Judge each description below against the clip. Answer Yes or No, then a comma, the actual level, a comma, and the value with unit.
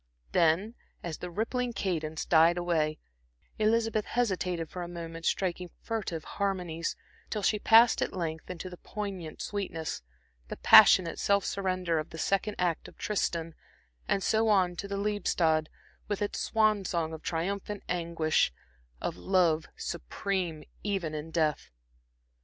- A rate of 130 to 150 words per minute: Yes, average, 140 wpm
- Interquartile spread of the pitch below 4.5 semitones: Yes, average, 3.6 semitones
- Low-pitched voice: No, medium, 180 Hz